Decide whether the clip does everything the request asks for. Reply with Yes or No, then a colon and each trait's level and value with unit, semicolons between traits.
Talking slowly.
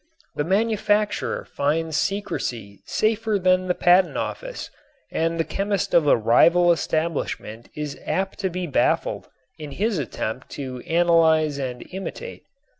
Yes: slow, 130 wpm